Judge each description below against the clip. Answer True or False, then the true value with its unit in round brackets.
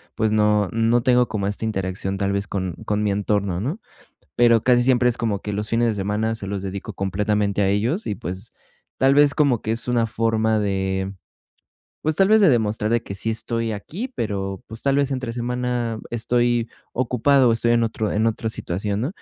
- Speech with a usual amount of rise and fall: True (3.1 semitones)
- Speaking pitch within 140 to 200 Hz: False (110 Hz)